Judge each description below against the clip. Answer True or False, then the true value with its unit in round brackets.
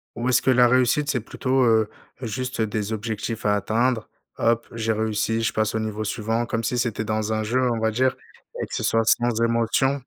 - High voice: False (115 Hz)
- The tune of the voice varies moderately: False (2.0 semitones)